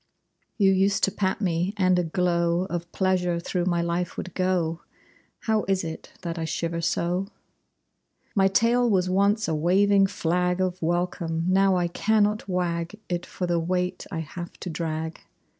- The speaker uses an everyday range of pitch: No, narrow, 2.2 semitones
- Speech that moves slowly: No, average, 165 wpm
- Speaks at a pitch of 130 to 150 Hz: No, medium, 180 Hz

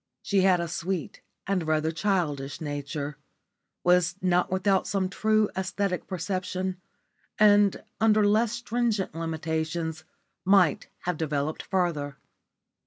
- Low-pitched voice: No, medium, 180 Hz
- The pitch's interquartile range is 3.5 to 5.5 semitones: Yes, average, 3.8 semitones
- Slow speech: Yes, slow, 110 wpm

